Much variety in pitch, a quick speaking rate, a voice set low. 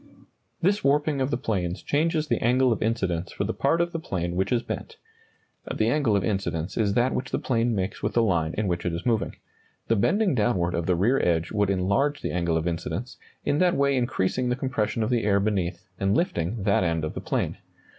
Yes: wide, 6.0 semitones; fast, 225 wpm; low, 110 Hz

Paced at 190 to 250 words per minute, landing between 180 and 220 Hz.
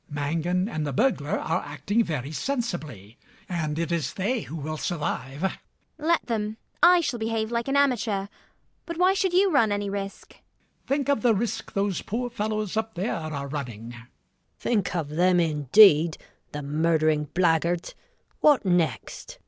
No: average, 165 wpm; medium, 185 Hz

